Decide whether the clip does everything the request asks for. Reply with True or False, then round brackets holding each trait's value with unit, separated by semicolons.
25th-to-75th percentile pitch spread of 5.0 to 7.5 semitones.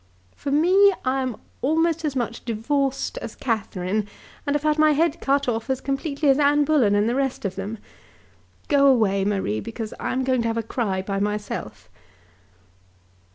True (5.4 semitones)